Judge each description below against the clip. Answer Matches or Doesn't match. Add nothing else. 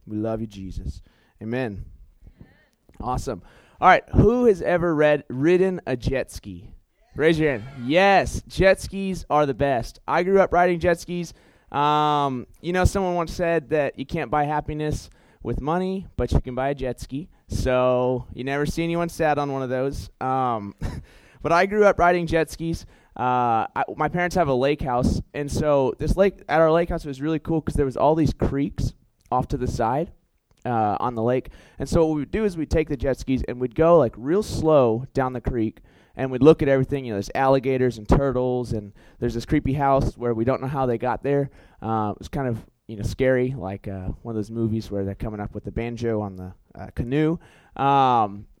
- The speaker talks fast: Matches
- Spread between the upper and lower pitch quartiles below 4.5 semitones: Doesn't match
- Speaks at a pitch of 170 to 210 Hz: Doesn't match